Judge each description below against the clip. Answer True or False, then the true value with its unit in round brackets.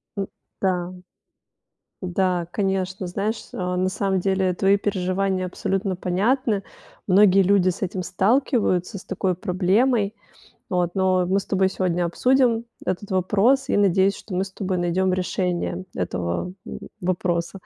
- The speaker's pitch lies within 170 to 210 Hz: True (190 Hz)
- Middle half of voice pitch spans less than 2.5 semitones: True (1.7 semitones)